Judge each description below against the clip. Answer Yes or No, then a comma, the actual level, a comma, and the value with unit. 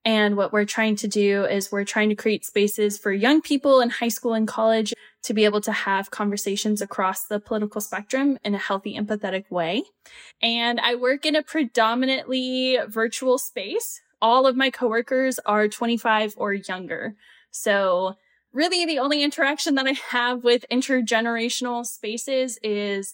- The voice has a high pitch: Yes, high, 225 Hz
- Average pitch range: Yes, average, 3.7 semitones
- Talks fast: No, average, 165 wpm